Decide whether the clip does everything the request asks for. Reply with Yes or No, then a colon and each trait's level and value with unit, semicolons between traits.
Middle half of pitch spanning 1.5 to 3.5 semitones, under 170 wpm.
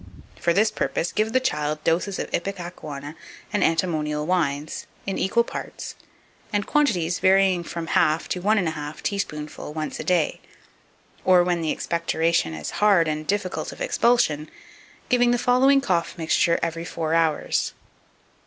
No: average, 4.3 semitones; average, 155 wpm